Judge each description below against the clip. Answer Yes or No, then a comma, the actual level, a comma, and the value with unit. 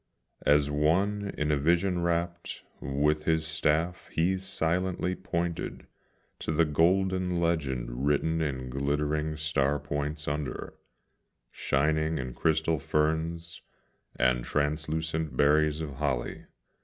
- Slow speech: Yes, slow, 110 wpm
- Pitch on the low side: Yes, very low, 75 Hz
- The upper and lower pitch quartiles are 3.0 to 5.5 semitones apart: No, narrow, 2.5 semitones